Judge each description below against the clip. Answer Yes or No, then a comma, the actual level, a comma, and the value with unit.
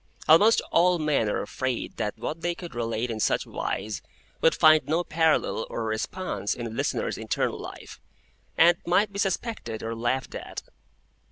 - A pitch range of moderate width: No, wide, 7.2 semitones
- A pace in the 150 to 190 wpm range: Yes, average, 165 wpm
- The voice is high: No, medium, 155 Hz